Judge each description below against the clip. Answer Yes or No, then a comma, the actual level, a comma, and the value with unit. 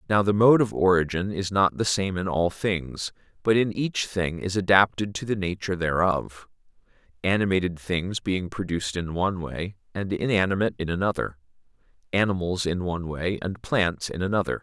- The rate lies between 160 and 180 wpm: Yes, average, 170 wpm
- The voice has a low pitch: Yes, very low, 95 Hz